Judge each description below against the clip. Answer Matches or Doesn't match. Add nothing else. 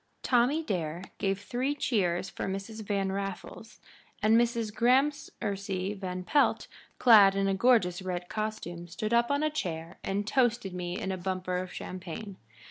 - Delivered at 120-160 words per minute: Matches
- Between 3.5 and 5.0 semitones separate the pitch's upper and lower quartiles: Matches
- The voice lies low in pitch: Doesn't match